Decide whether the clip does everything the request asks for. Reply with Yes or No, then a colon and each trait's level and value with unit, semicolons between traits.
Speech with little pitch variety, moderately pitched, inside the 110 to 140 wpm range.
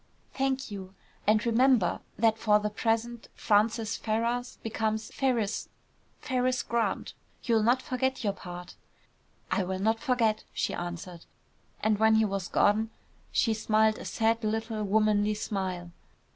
No: narrow, 2.0 semitones; high, 220 Hz; slow, 135 wpm